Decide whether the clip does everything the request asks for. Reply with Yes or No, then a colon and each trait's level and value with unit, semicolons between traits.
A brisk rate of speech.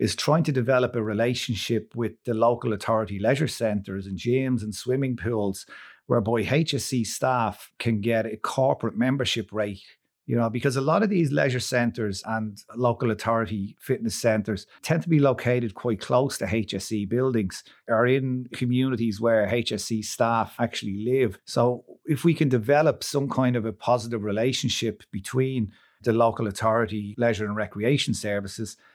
No: average, 160 wpm